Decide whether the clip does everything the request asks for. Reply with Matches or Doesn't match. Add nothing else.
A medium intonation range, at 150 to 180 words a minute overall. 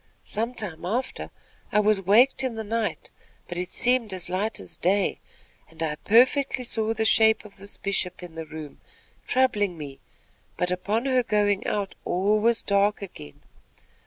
Matches